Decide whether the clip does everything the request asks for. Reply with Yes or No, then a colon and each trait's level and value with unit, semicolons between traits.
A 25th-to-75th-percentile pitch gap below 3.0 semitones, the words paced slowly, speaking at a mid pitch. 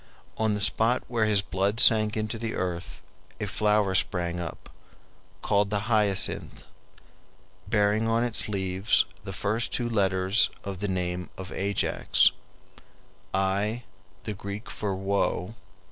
No: narrow, 2.4 semitones; slow, 130 wpm; low, 100 Hz